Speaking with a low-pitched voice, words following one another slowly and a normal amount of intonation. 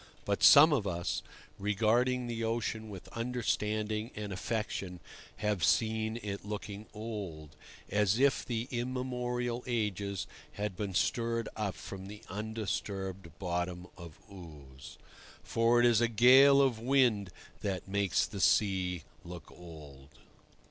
Yes: low, 105 Hz; slow, 125 wpm; average, 3.7 semitones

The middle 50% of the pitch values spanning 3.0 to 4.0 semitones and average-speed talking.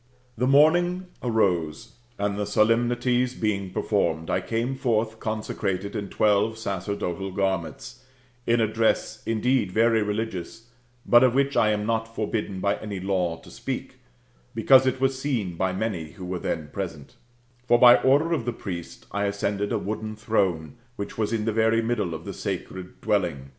Yes: average, 3.4 semitones; average, 170 wpm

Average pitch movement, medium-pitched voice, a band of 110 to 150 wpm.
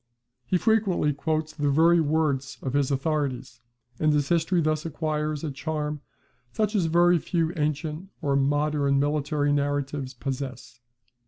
No: narrow, 2.3 semitones; medium, 150 Hz; average, 140 wpm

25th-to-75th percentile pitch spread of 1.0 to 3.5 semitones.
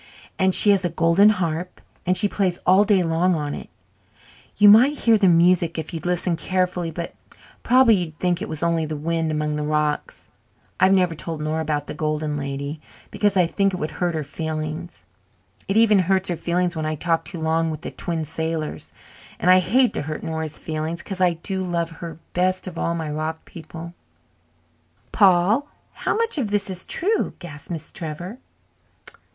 Yes: average, 2.9 semitones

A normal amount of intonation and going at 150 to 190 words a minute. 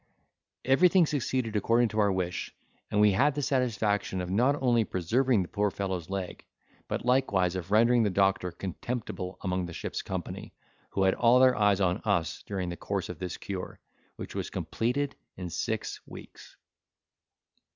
Yes: average, 4.8 semitones; average, 165 wpm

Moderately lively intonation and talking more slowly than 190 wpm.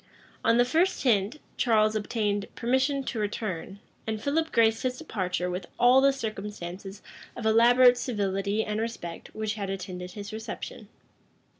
Yes: average, 3.5 semitones; average, 145 wpm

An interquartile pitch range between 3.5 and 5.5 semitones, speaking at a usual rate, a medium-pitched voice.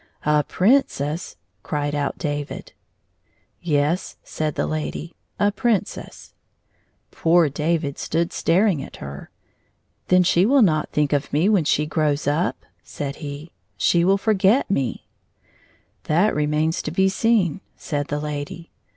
Yes: average, 3.9 semitones; average, 155 wpm; medium, 155 Hz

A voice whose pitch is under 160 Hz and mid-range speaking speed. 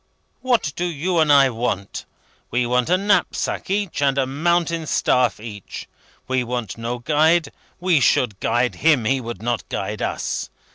Yes: low, 135 Hz; average, 160 wpm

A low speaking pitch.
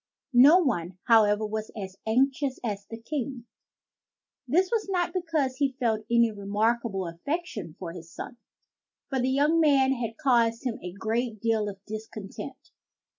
No: high, 235 Hz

